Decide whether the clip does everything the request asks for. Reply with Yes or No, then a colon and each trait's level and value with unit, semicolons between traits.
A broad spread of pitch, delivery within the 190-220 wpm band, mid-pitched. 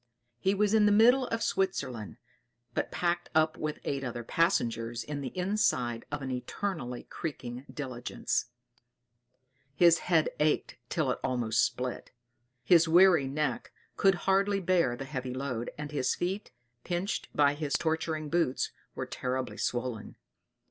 No: wide, 5.9 semitones; average, 140 wpm; medium, 150 Hz